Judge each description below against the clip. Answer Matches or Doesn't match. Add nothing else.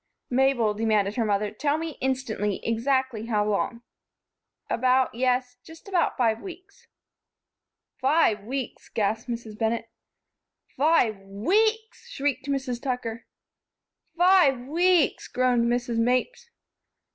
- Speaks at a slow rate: Matches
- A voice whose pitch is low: Doesn't match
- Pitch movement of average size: Matches